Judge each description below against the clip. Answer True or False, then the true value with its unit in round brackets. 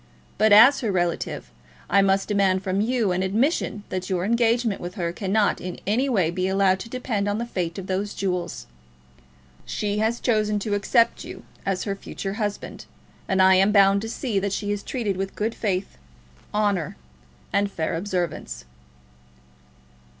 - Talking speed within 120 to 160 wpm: False (170 wpm)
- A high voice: True (200 Hz)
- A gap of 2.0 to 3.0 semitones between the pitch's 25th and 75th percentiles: True (2.4 semitones)